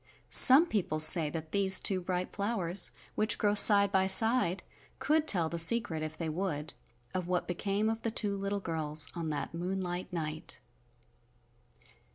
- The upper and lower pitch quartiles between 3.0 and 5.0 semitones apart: Yes, average, 3.8 semitones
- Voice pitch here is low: No, medium, 185 Hz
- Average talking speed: Yes, average, 160 wpm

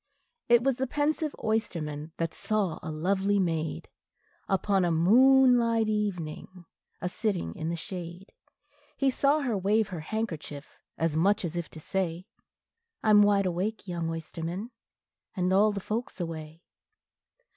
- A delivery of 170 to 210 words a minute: No, average, 145 wpm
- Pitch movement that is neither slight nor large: Yes, average, 4.8 semitones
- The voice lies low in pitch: No, high, 190 Hz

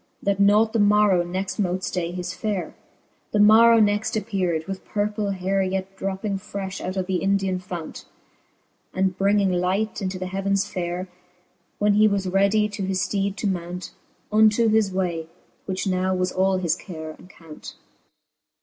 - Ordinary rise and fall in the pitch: No, narrow, 2.0 semitones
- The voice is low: No, high, 195 Hz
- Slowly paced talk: No, average, 165 wpm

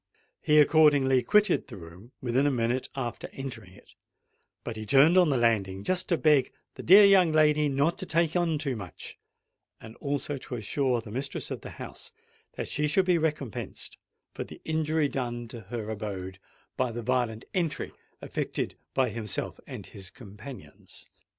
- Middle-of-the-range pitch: No, low, 130 Hz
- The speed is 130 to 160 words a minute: No, average, 170 wpm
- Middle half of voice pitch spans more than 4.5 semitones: Yes, average, 5.3 semitones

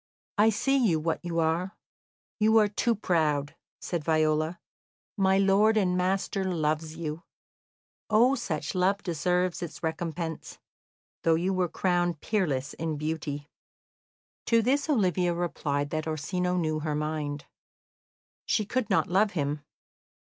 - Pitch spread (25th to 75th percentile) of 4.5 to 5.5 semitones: No, average, 3.8 semitones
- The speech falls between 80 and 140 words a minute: Yes, slow, 135 wpm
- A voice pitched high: No, medium, 175 Hz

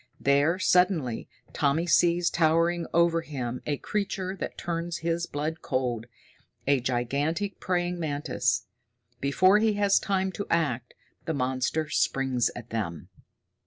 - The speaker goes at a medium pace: No, slow, 125 wpm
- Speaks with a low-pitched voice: No, medium, 160 Hz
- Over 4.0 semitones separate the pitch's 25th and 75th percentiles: Yes, average, 4.8 semitones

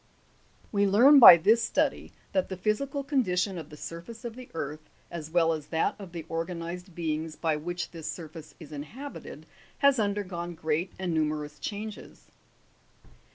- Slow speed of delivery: No, average, 165 wpm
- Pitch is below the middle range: No, medium, 175 Hz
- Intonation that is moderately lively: Yes, average, 4.9 semitones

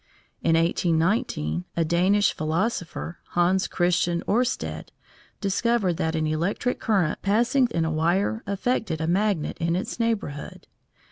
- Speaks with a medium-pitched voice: Yes, medium, 180 Hz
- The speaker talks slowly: Yes, slow, 125 wpm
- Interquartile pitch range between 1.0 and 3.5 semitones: No, average, 4.5 semitones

